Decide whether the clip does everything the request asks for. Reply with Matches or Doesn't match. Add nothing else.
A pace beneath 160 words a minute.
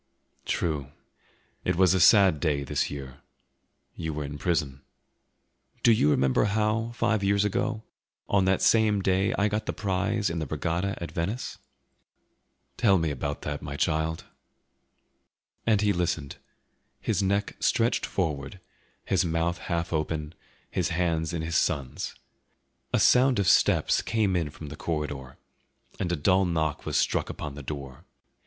Matches